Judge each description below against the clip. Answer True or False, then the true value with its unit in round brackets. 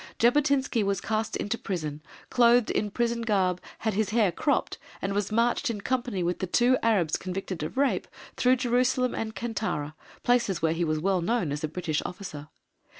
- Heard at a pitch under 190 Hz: False (210 Hz)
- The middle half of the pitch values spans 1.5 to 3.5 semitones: False (5.1 semitones)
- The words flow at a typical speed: True (180 wpm)